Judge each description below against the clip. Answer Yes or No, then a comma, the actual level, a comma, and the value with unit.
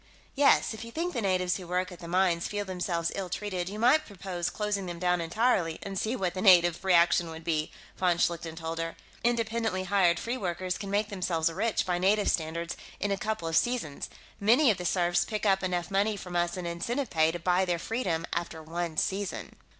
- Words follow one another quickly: Yes, fast, 210 wpm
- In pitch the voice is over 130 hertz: Yes, medium, 185 Hz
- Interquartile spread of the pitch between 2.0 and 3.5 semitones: Yes, average, 3.2 semitones